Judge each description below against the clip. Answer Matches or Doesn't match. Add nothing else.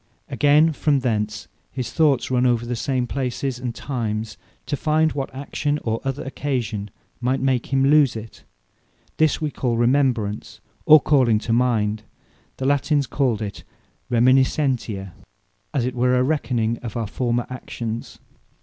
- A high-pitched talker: Doesn't match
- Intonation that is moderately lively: Matches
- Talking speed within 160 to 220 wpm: Doesn't match